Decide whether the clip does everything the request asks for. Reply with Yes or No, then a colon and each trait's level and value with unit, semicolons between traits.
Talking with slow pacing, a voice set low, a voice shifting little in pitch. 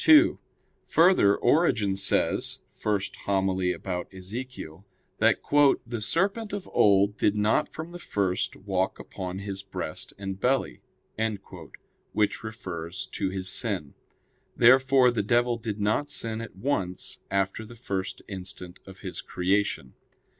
No: slow, 130 wpm; low, 100 Hz; average, 4.2 semitones